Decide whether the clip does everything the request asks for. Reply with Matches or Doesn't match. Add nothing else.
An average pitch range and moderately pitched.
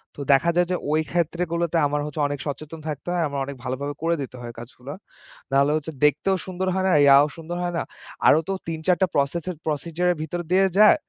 Matches